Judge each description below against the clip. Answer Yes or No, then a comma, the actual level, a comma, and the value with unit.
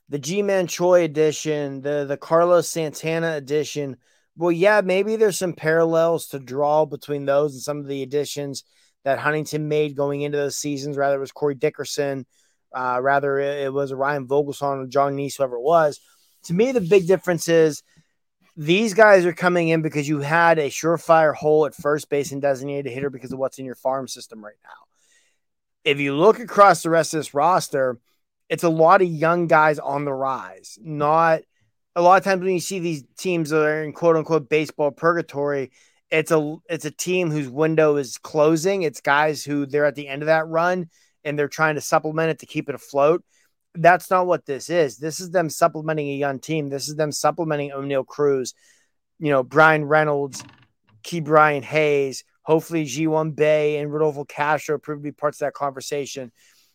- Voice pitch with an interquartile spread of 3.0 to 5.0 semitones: No, narrow, 2.6 semitones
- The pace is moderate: Yes, average, 195 wpm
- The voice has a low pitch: No, medium, 150 Hz